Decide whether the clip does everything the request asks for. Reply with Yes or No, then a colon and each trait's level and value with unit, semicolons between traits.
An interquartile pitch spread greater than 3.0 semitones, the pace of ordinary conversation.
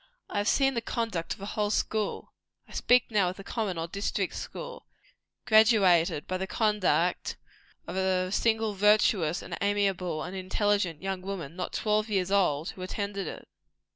No: average, 2.7 semitones; average, 170 wpm